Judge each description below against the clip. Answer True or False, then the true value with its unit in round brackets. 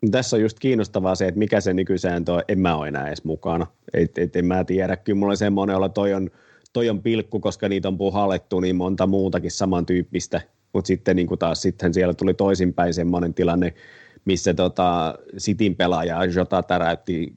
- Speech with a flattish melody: True (1.9 semitones)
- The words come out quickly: True (195 wpm)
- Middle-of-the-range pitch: False (95 Hz)